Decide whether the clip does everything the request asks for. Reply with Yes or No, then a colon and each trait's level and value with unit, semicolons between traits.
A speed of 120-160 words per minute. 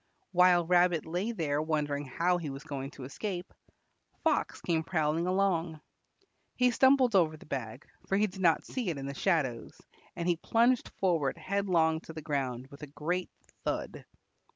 No: average, 170 wpm